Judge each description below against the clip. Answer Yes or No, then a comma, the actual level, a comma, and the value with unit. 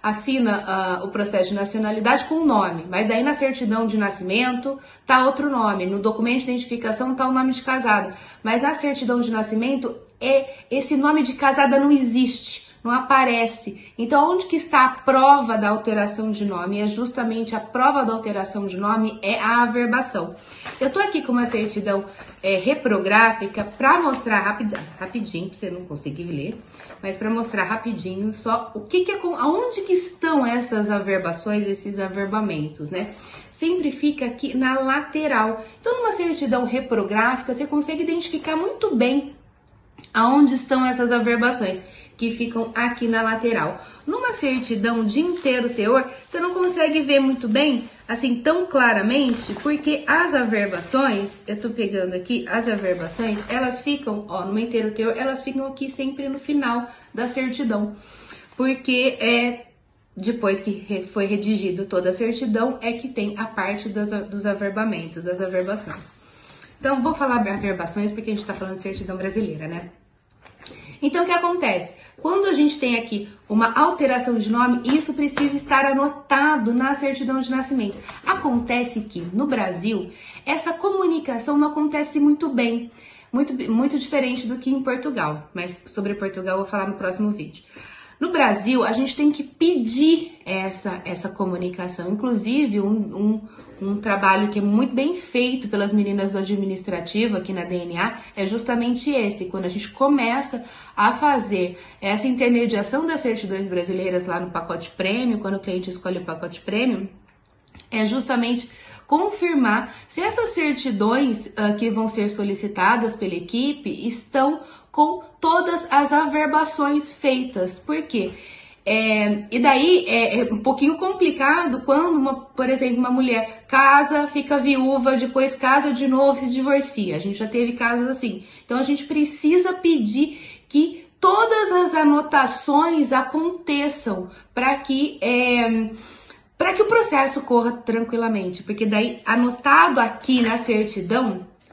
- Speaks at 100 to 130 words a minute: No, average, 155 wpm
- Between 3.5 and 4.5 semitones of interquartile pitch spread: No, average, 5.0 semitones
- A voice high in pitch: Yes, high, 240 Hz